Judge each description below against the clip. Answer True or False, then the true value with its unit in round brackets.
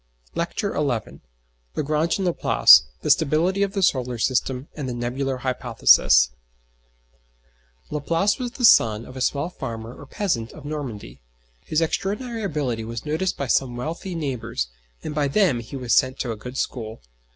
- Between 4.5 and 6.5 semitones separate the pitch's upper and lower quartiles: True (5.6 semitones)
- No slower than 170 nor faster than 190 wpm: False (160 wpm)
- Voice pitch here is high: False (135 Hz)